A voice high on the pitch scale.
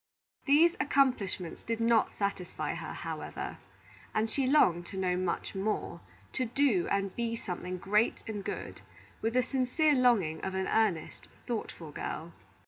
Yes: high, 215 Hz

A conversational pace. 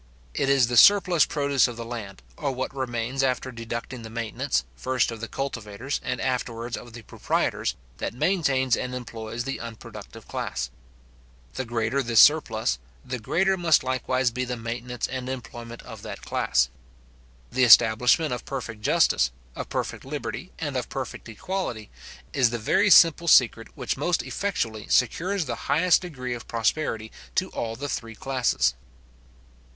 Yes: average, 155 wpm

